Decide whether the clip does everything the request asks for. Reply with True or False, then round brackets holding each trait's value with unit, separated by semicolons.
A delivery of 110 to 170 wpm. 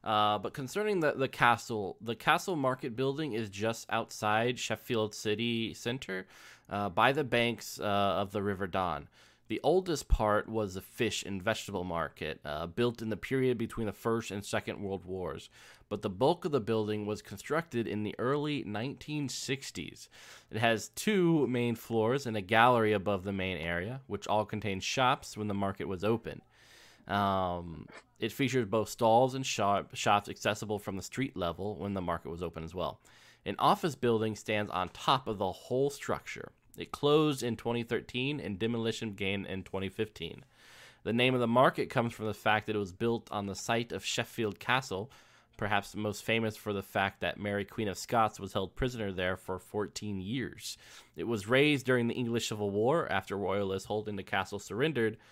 False (185 wpm)